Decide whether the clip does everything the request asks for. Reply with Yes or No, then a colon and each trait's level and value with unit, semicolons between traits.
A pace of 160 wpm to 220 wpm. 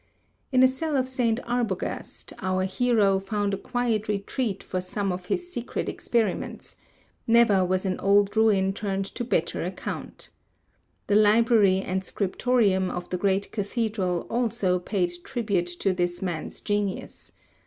No: average, 145 wpm